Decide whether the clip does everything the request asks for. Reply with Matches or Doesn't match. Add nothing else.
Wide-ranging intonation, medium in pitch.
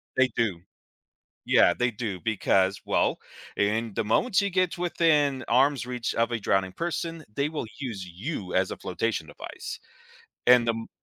Doesn't match